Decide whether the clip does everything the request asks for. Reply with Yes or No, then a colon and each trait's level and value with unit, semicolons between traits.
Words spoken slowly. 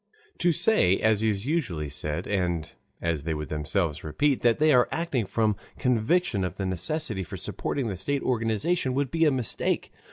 No: average, 180 wpm